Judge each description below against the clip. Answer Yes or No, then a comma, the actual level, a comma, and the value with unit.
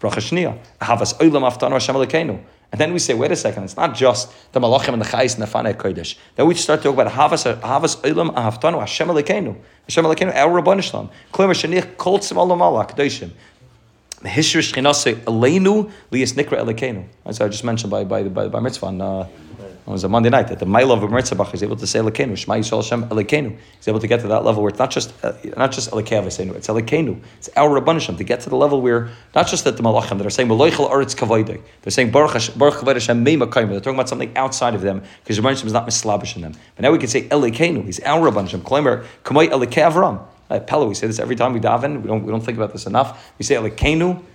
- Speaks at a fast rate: Yes, fast, 210 wpm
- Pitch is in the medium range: No, low, 120 Hz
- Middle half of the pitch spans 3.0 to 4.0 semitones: No, average, 4.7 semitones